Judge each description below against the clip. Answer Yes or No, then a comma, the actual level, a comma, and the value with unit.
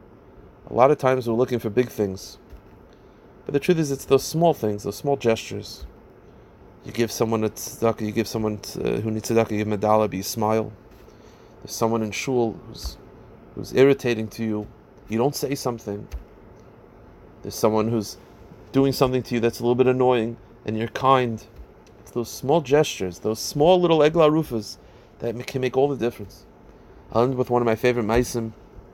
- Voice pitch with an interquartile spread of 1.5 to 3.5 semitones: Yes, average, 3.0 semitones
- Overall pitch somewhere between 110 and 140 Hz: Yes, low, 115 Hz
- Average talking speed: Yes, average, 185 wpm